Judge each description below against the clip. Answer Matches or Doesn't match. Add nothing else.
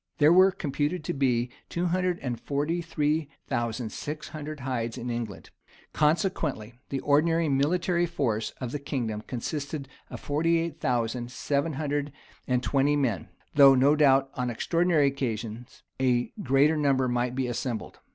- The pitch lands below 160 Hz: Matches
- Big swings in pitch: Doesn't match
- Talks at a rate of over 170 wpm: Doesn't match